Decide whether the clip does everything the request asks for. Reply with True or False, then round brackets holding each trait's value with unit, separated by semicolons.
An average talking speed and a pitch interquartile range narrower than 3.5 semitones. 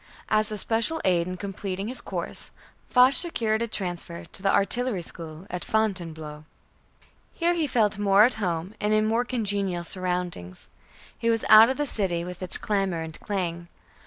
False (170 wpm; 4.0 semitones)